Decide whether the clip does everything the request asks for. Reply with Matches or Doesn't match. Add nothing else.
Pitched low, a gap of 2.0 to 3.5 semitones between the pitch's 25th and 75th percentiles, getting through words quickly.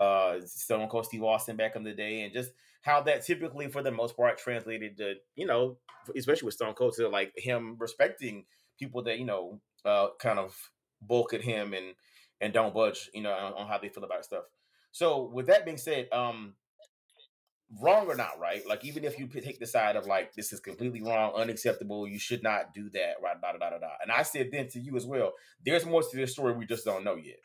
Doesn't match